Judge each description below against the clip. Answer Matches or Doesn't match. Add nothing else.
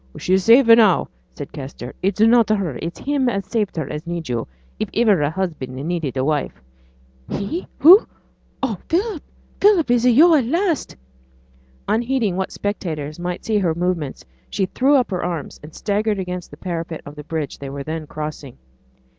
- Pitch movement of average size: Doesn't match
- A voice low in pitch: Doesn't match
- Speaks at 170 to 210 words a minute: Matches